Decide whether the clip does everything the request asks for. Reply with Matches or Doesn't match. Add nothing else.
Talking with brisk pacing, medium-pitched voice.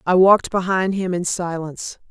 Doesn't match